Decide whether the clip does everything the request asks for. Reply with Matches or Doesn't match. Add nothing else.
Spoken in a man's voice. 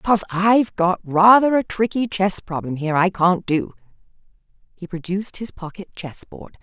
Doesn't match